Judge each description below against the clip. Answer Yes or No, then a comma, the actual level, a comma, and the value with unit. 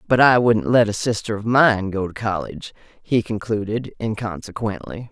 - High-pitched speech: No, low, 110 Hz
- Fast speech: No, average, 165 wpm